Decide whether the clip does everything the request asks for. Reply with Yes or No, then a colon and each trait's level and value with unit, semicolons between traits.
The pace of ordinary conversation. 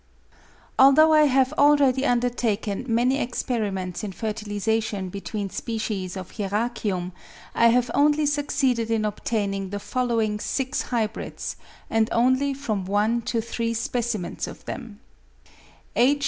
No: slow, 120 wpm